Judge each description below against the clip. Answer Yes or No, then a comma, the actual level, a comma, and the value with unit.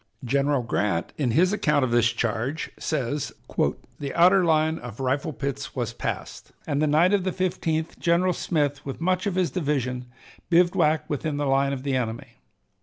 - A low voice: No, medium, 145 Hz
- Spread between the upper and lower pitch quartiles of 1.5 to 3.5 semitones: No, average, 4.5 semitones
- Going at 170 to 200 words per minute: Yes, average, 175 wpm